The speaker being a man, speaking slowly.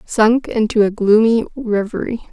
No: female; slow, 130 wpm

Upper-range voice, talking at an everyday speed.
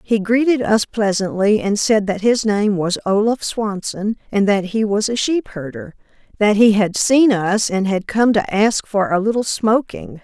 Yes: high, 210 Hz; average, 195 wpm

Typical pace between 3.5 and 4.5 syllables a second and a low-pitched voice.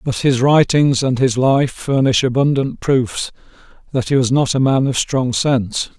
Yes: 4.4 syllables/s; low, 130 Hz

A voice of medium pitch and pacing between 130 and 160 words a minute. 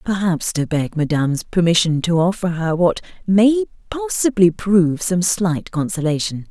Yes: medium, 180 Hz; average, 140 wpm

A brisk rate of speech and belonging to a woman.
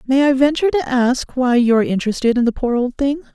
Yes: fast, 250 wpm; female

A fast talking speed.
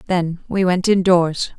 No: average, 150 wpm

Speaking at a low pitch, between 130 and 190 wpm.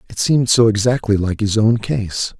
No: low, 110 Hz; average, 200 wpm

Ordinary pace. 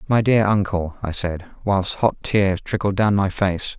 Yes: average, 190 wpm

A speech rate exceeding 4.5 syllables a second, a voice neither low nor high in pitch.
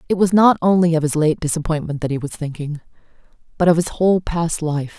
Yes: 6.0 syllables/s; medium, 165 Hz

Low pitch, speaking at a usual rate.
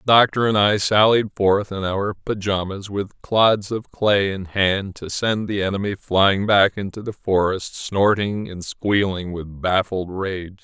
Yes: low, 100 Hz; average, 170 wpm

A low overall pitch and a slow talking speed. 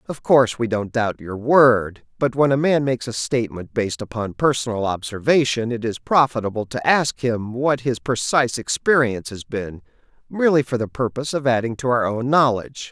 No: low, 125 Hz; average, 185 wpm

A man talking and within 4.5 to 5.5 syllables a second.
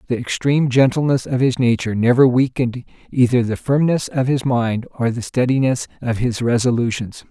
Yes: male; 5.4 syllables/s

